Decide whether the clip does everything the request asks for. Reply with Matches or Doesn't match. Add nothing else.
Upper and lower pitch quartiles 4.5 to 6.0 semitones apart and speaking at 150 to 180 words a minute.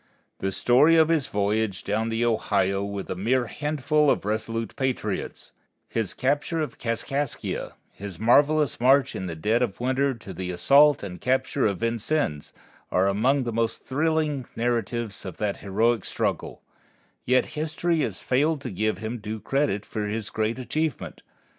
Matches